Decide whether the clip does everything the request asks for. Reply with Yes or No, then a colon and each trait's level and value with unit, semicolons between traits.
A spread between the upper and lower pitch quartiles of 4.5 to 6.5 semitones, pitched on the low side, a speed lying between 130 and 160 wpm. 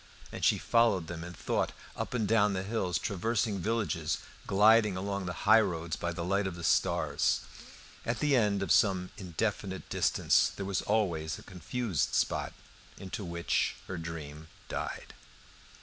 No: average, 3.9 semitones; very low, 95 Hz; average, 155 wpm